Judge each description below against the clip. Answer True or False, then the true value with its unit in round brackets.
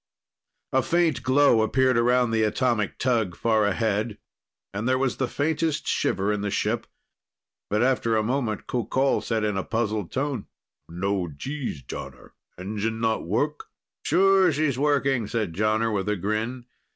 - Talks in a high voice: False (115 Hz)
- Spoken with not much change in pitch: False (4.0 semitones)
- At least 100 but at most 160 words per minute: True (150 wpm)